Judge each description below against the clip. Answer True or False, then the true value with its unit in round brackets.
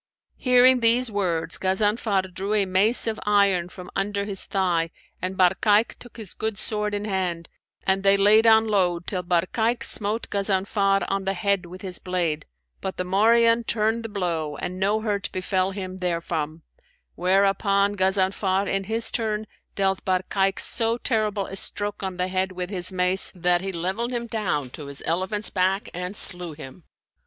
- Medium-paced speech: True (170 wpm)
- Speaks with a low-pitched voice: False (195 Hz)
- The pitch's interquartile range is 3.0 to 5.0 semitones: False (2.5 semitones)